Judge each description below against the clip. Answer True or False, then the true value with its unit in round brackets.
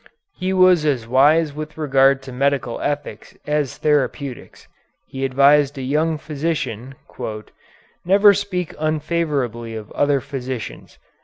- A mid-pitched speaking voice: True (145 Hz)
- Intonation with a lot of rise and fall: False (2.8 semitones)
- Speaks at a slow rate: True (120 wpm)